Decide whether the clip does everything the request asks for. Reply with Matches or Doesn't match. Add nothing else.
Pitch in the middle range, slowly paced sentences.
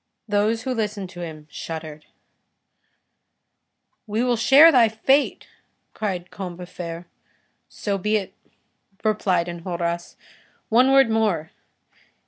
Doesn't match